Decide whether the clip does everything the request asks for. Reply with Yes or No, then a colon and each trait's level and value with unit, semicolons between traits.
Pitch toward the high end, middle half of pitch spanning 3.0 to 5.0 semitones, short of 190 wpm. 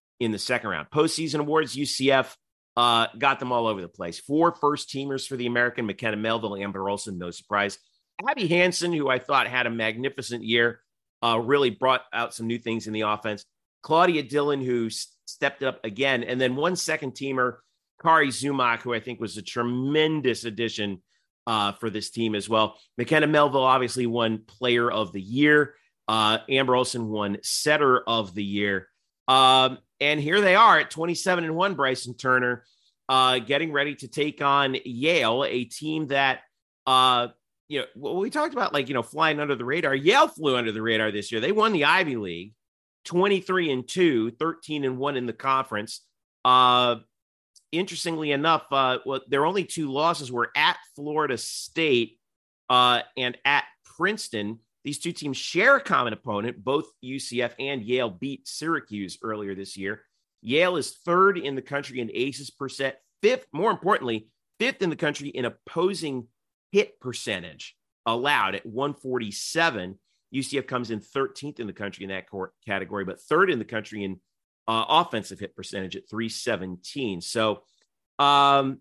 No: low, 125 Hz; average, 4.5 semitones; average, 170 wpm